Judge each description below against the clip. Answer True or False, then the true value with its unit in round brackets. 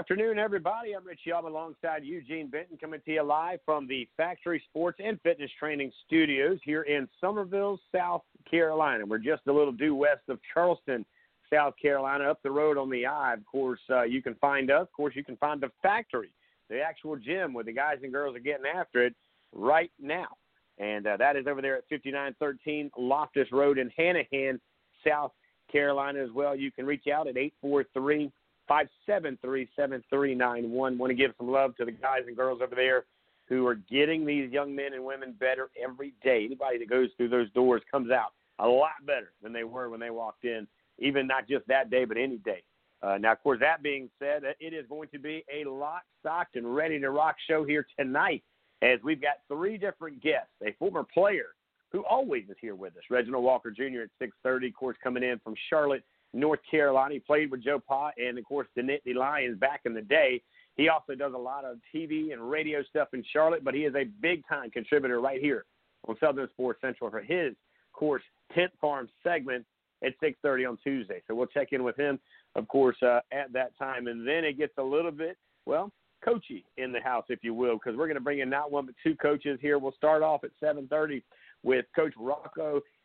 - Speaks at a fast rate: True (210 wpm)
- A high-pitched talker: False (140 Hz)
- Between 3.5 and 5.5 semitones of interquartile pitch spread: False (3.1 semitones)